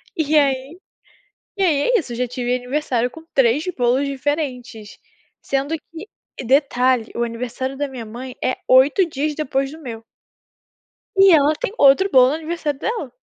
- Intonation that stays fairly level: No, average, 3.5 semitones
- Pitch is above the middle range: Yes, very high, 270 Hz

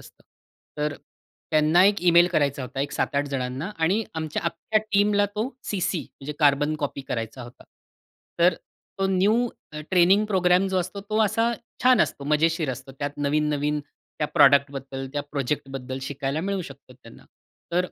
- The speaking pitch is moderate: Yes, medium, 150 Hz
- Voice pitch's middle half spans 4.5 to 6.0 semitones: Yes, average, 5.3 semitones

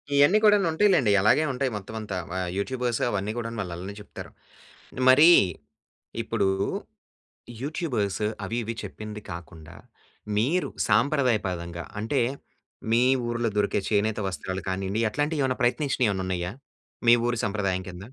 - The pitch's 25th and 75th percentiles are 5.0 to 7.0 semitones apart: Yes, average, 5.3 semitones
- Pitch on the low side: Yes, low, 110 Hz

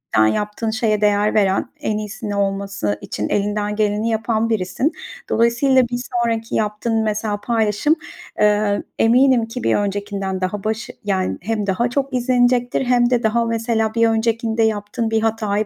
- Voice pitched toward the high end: Yes, high, 220 Hz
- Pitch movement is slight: Yes, narrow, 2.1 semitones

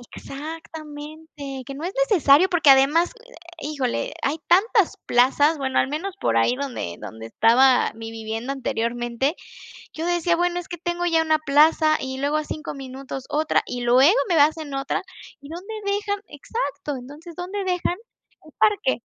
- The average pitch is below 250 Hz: No, very high, 295 Hz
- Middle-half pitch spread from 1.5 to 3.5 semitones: No, average, 4.5 semitones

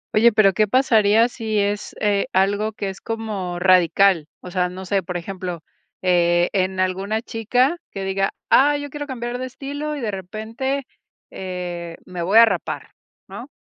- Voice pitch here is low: No, high, 200 Hz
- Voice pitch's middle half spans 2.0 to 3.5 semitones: No, average, 3.9 semitones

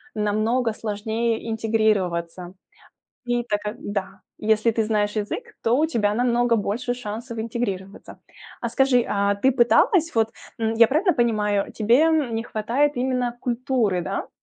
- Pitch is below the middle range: No, high, 225 Hz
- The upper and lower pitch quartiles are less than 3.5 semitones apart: Yes, average, 2.8 semitones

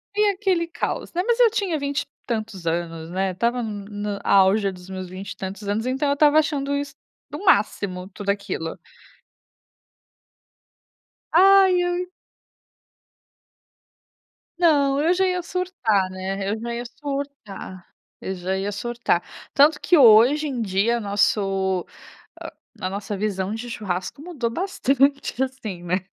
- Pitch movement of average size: No, wide, 7.1 semitones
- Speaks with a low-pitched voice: No, high, 225 Hz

